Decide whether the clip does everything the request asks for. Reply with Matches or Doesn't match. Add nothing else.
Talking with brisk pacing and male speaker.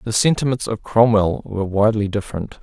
Doesn't match